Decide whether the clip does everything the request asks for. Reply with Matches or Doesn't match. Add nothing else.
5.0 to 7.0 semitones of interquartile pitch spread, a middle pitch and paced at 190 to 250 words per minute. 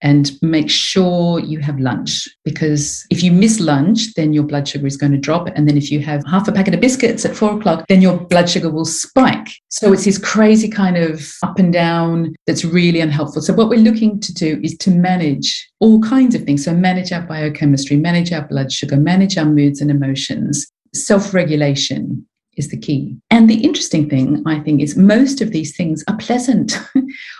Matches